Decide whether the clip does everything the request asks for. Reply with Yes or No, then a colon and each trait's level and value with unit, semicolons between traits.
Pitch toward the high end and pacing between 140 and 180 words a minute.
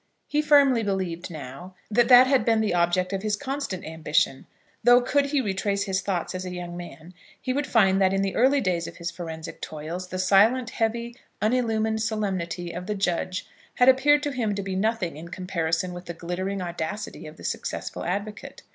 No: high, 195 Hz; average, 195 wpm